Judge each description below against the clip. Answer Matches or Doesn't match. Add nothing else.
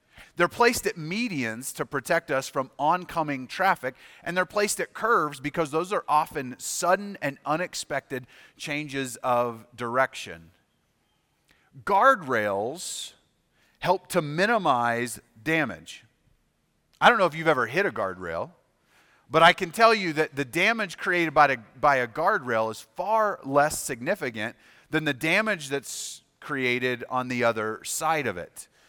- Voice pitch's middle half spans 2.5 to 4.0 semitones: Doesn't match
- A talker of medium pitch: Matches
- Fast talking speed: Doesn't match